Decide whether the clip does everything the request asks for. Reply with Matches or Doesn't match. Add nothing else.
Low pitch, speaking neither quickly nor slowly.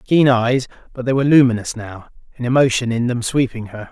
Matches